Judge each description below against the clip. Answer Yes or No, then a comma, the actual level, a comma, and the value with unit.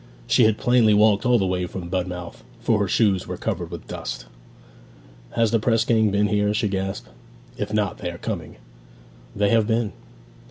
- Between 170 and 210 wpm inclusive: Yes, average, 185 wpm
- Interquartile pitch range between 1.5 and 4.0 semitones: Yes, average, 2.8 semitones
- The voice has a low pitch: Yes, low, 105 Hz